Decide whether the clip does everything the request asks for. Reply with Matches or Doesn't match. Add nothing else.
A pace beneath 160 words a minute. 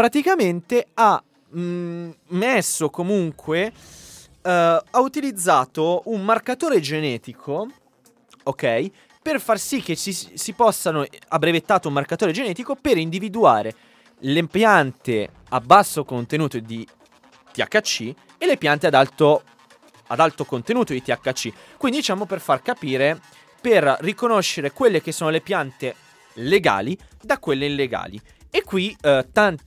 Matches